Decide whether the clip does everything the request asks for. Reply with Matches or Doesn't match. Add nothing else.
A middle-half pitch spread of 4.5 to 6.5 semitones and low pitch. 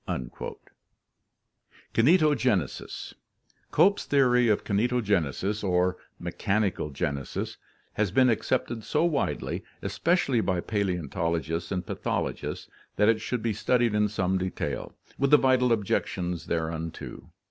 Matches